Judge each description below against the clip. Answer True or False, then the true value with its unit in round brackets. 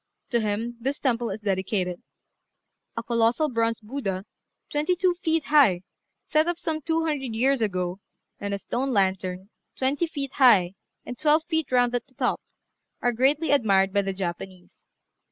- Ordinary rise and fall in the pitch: False (6.5 semitones)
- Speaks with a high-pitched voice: True (240 Hz)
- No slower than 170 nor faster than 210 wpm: False (160 wpm)